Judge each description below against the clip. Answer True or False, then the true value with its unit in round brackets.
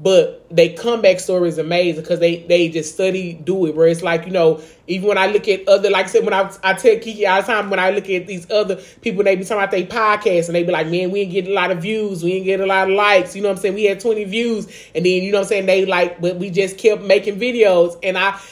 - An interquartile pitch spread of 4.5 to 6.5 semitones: False (2.5 semitones)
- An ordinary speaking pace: False (300 wpm)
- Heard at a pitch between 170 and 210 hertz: True (190 Hz)